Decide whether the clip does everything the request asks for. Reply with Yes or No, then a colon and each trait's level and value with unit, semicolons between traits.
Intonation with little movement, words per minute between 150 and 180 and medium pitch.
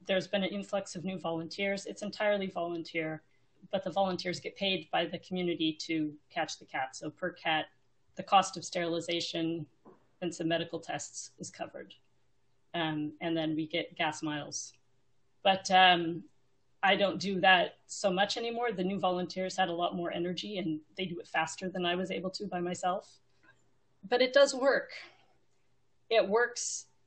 No: average, 3.4 semitones; average, 170 wpm; medium, 170 Hz